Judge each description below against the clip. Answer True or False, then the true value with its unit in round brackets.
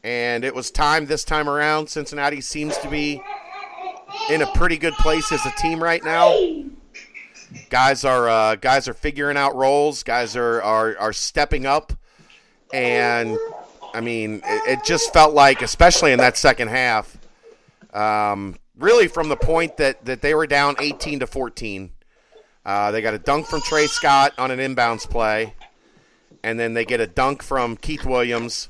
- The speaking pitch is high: False (140 Hz)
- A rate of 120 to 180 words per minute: True (170 wpm)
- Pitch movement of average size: True (4.9 semitones)